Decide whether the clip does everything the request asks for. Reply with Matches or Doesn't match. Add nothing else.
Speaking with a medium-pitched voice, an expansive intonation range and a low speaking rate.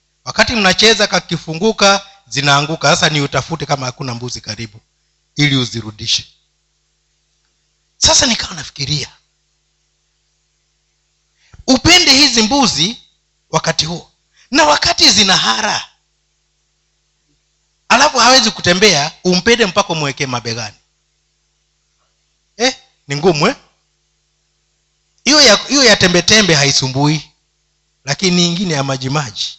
Matches